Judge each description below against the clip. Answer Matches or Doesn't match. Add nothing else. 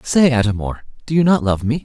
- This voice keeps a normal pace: Doesn't match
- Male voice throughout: Matches